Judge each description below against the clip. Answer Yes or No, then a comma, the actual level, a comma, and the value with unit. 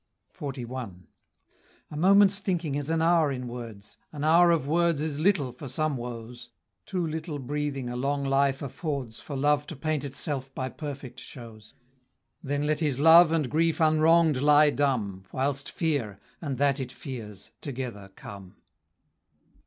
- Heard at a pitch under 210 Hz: Yes, medium, 140 Hz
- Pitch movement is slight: No, average, 3.8 semitones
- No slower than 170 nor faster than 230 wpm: No, average, 155 wpm